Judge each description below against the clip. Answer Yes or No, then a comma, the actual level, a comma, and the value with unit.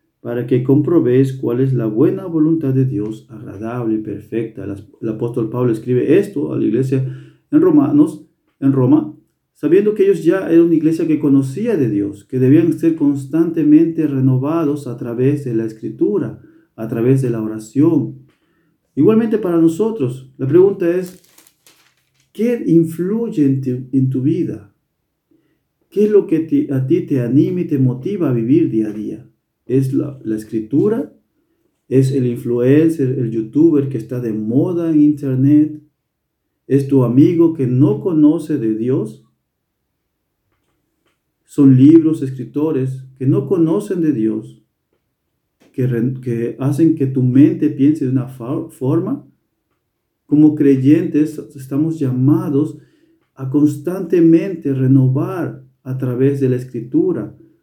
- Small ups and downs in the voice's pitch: No, average, 4.2 semitones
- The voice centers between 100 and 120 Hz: No, medium, 140 Hz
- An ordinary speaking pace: Yes, average, 140 wpm